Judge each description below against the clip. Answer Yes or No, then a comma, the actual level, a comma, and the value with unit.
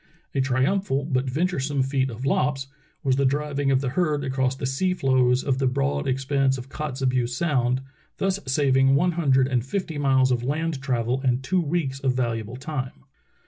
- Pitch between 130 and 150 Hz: Yes, low, 135 Hz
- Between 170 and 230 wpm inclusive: Yes, average, 180 wpm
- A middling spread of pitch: No, narrow, 2.0 semitones